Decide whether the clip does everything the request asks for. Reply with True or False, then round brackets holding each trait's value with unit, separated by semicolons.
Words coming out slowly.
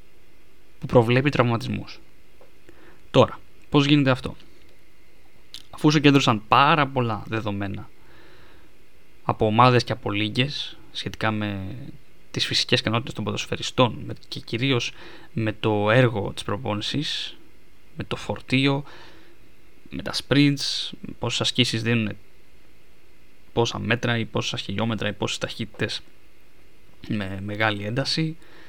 True (105 wpm)